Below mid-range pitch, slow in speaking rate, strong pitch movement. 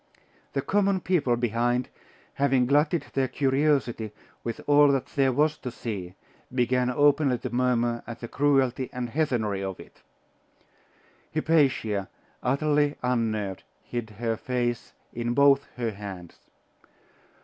No: low, 125 Hz; slow, 125 wpm; average, 3.4 semitones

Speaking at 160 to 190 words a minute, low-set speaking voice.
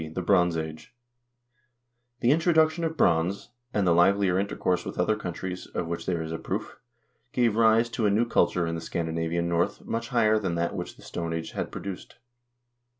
Yes: average, 185 wpm; very low, 90 Hz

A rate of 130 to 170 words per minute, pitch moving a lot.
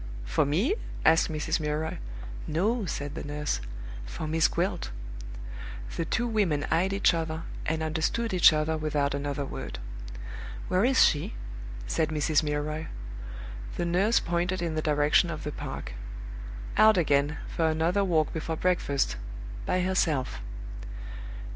No: slow, 135 wpm; average, 3.2 semitones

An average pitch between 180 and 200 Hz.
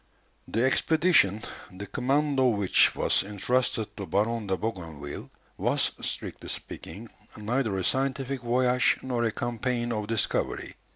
No: low, 115 Hz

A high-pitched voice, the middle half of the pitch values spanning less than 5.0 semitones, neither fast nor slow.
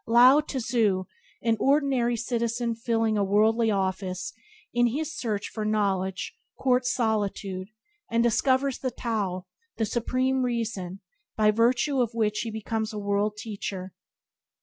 No: high, 225 Hz; average, 2.9 semitones; slow, 125 wpm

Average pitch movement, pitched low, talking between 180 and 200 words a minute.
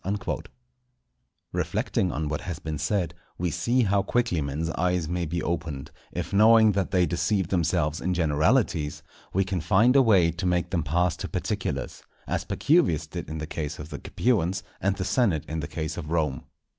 Yes: average, 3.8 semitones; very low, 85 Hz; average, 185 wpm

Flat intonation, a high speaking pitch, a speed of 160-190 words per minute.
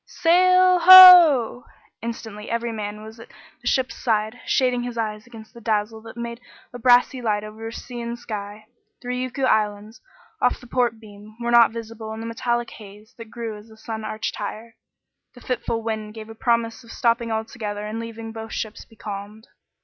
Yes: narrow, 1.8 semitones; high, 225 Hz; average, 180 wpm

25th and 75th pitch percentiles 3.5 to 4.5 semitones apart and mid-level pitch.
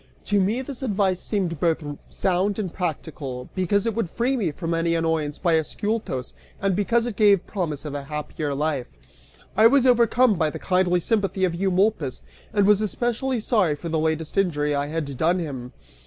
No: average, 5.0 semitones; medium, 180 Hz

